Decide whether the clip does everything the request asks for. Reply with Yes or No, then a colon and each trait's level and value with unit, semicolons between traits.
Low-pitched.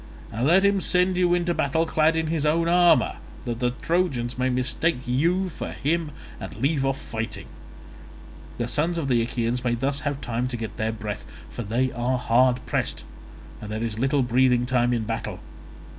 Yes: low, 130 Hz